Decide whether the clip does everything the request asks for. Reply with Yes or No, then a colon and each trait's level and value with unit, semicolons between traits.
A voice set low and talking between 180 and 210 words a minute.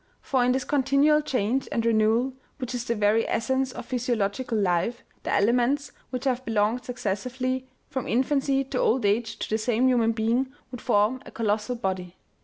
No: high, 245 Hz; average, 185 wpm